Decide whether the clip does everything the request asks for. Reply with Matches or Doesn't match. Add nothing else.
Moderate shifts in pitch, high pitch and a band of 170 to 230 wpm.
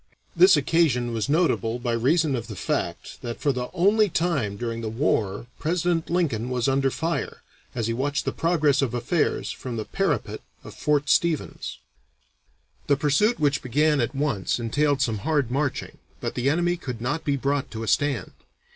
Doesn't match